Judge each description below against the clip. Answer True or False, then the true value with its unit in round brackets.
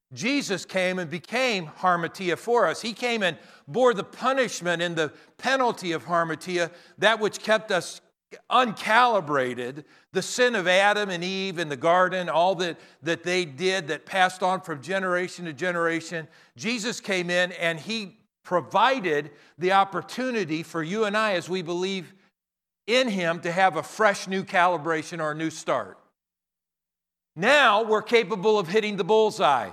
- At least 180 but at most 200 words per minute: False (155 wpm)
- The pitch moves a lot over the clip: False (4.1 semitones)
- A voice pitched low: False (185 Hz)